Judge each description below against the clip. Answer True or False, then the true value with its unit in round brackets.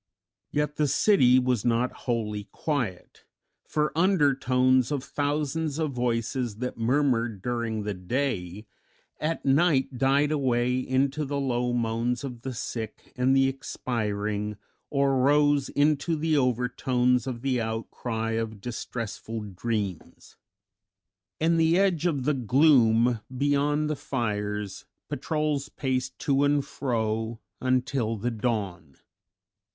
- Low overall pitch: True (125 Hz)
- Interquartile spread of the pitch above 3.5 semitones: True (3.9 semitones)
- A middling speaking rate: False (120 wpm)